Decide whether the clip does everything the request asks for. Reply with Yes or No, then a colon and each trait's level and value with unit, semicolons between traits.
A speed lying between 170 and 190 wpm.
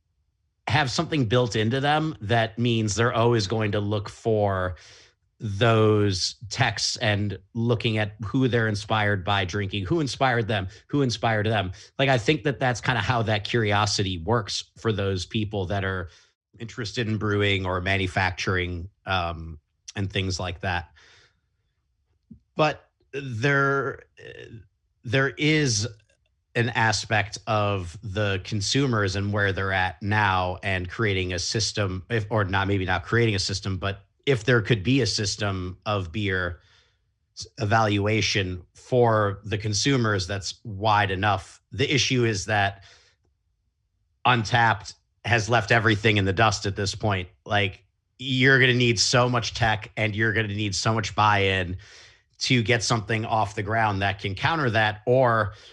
No: average, 150 wpm